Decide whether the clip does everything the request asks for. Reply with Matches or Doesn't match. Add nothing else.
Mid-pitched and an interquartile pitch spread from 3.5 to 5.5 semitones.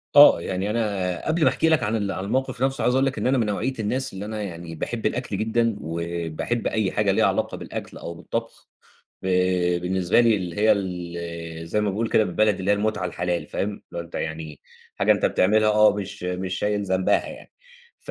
Doesn't match